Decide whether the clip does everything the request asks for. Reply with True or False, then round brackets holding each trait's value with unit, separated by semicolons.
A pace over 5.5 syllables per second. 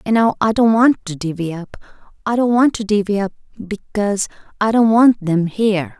False (5.1 syllables/s)